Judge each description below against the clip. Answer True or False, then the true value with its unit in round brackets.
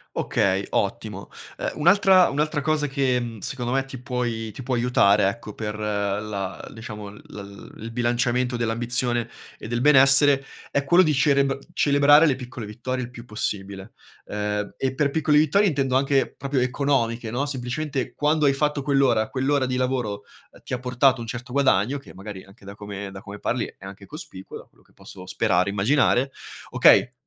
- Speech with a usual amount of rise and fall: True (4.5 semitones)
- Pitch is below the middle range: True (125 Hz)